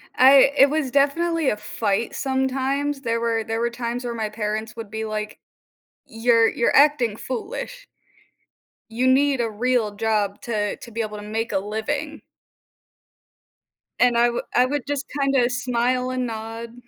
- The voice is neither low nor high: No, high, 235 Hz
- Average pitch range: Yes, average, 3.2 semitones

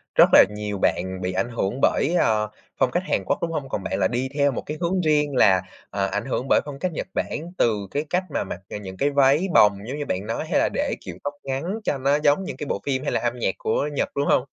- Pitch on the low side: Yes, low, 130 Hz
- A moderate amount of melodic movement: No, wide, 5.9 semitones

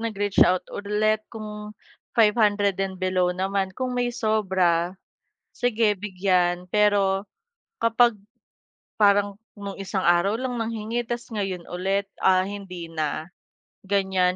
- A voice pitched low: No, high, 200 Hz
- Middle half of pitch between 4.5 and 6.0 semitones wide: No, narrow, 2.5 semitones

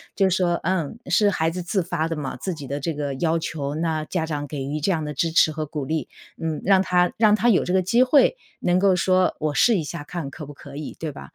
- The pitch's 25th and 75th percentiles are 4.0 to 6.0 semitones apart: No, average, 3.6 semitones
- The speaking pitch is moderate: Yes, medium, 165 Hz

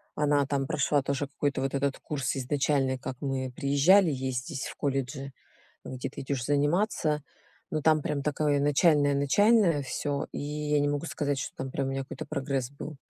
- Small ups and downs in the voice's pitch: Yes, narrow, 1.7 semitones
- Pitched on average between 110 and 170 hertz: Yes, medium, 140 Hz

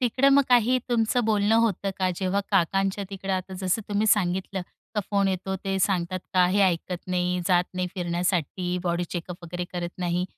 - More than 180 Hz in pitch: Yes, high, 190 Hz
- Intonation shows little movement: Yes, narrow, 2.3 semitones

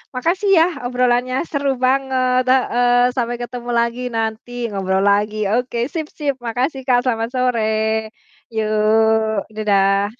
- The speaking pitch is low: No, high, 240 Hz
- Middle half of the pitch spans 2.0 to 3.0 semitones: Yes, average, 2.7 semitones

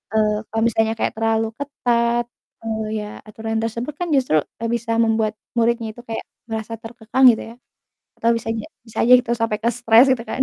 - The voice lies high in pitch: Yes, high, 225 Hz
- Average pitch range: No, narrow, 1.2 semitones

